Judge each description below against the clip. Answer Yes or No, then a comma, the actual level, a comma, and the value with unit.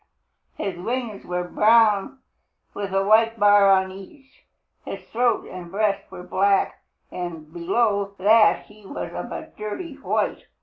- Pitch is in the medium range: No, high, 200 Hz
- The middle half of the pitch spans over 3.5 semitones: No, average, 2.9 semitones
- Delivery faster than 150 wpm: No, average, 140 wpm